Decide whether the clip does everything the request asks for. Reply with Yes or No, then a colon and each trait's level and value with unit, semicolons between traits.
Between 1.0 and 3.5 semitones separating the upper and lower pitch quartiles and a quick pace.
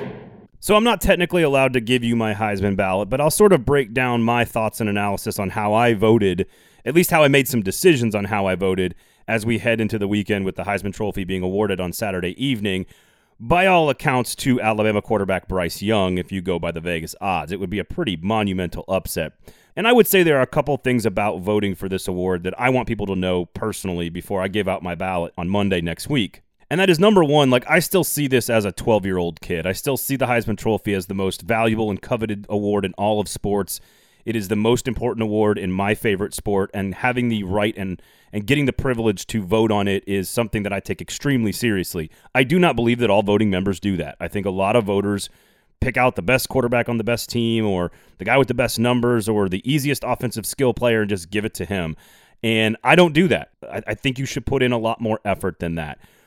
No: average, 4.2 semitones; fast, 245 wpm